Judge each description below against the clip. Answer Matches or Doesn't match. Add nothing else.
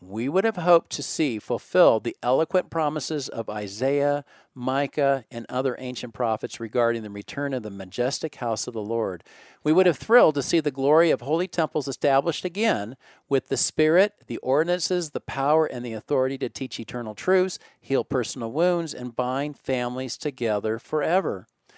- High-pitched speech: Doesn't match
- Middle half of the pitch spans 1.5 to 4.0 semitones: Doesn't match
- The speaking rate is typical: Matches